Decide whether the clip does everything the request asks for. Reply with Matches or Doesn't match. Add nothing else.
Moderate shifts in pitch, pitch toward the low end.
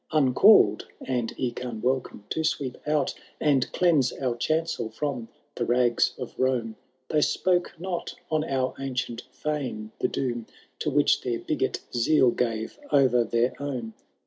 Matches